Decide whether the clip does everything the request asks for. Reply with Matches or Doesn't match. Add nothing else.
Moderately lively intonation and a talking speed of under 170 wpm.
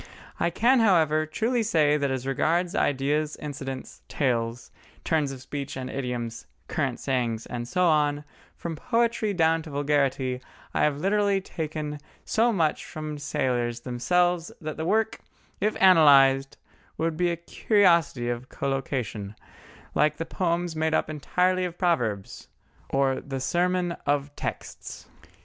Matches